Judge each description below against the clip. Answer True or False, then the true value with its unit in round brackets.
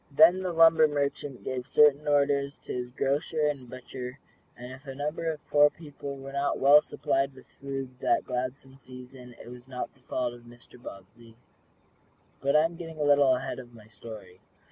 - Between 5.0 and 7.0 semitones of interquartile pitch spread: False (2.8 semitones)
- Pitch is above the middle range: False (135 Hz)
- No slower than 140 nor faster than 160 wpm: False (190 wpm)